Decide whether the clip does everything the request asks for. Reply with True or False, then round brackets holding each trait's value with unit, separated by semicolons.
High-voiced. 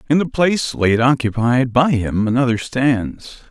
False (125 Hz)